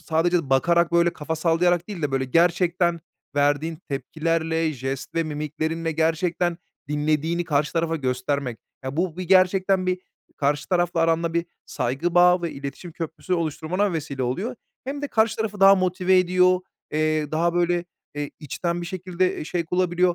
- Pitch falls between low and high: Yes, medium, 170 Hz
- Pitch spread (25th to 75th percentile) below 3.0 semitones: Yes, narrow, 2.6 semitones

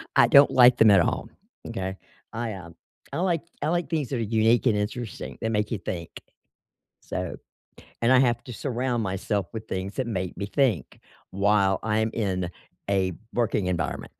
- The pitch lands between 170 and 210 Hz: No, low, 110 Hz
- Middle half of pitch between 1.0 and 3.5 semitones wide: No, average, 4.1 semitones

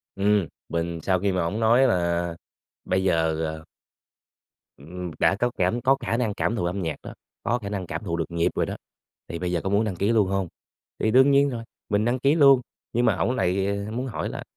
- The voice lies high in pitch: No, low, 100 Hz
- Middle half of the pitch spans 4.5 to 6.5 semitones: Yes, average, 5.1 semitones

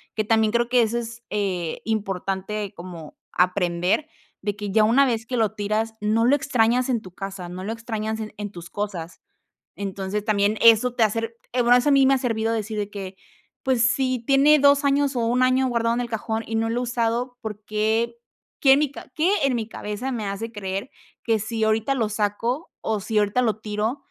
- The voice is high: Yes, high, 225 Hz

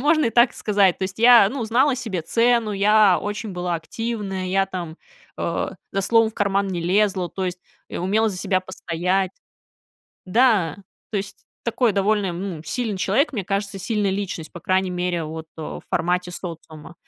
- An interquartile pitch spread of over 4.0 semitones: No, average, 3.2 semitones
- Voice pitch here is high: Yes, high, 195 Hz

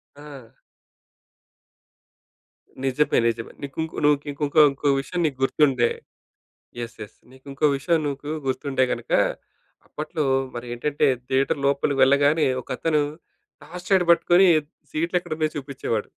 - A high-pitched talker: No, medium, 145 Hz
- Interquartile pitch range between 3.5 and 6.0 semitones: No, average, 2.7 semitones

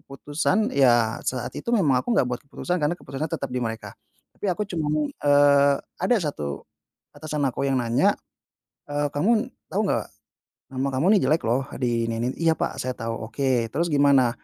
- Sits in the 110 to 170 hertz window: Yes, medium, 140 Hz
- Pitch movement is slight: No, average, 4.0 semitones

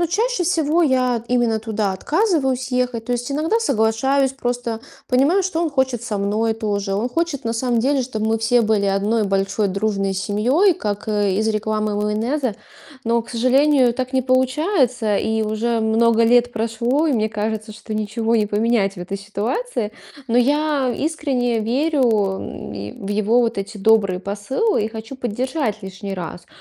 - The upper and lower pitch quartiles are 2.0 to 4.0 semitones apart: Yes, average, 3.7 semitones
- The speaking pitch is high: Yes, high, 230 Hz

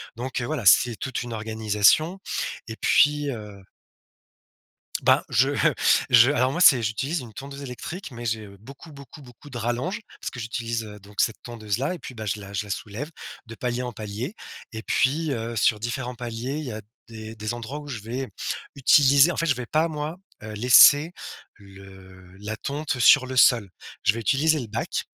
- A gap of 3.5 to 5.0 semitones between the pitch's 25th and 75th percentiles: Yes, average, 4.3 semitones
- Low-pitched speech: Yes, low, 120 Hz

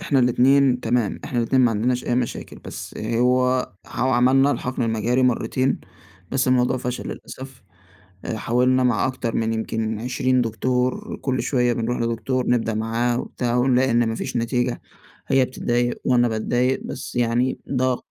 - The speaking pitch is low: Yes, low, 125 Hz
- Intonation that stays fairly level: Yes, narrow, 1.7 semitones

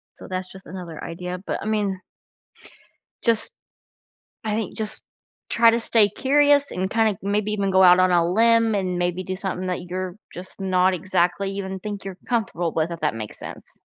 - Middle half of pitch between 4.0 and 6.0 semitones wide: No, average, 2.9 semitones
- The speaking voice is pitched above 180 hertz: Yes, high, 190 Hz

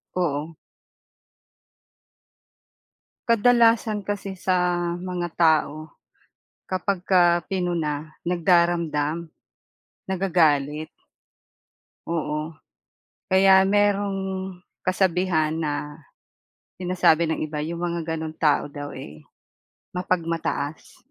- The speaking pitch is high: No, medium, 170 Hz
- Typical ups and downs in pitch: Yes, average, 3.3 semitones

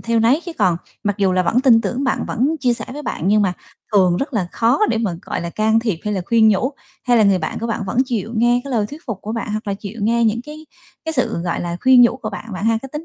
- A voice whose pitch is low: No, high, 225 Hz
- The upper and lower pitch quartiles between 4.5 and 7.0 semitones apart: No, average, 3.6 semitones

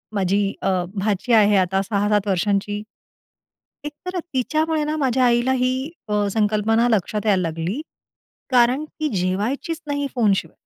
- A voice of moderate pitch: No, high, 215 Hz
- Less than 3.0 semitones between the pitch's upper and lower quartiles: No, average, 4.6 semitones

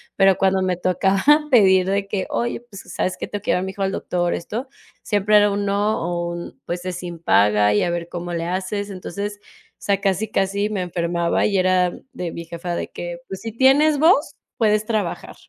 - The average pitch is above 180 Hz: Yes, high, 190 Hz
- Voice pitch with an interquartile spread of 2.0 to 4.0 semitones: Yes, average, 2.8 semitones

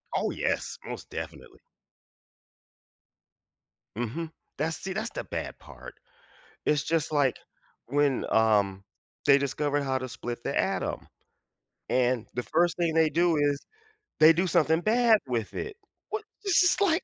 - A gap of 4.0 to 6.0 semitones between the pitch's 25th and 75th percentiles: Yes, average, 5.1 semitones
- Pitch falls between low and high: Yes, medium, 150 Hz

